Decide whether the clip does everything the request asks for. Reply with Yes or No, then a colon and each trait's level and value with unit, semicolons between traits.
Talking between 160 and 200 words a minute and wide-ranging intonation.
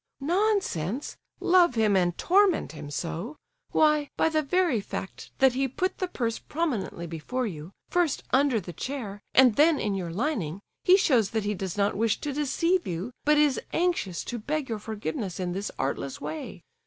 Yes: average, 180 wpm; wide, 8.2 semitones